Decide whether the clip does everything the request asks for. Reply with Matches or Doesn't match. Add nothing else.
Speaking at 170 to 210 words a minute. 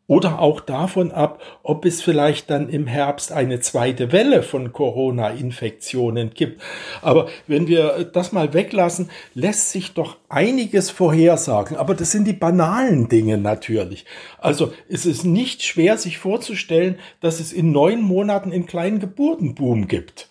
Doesn't match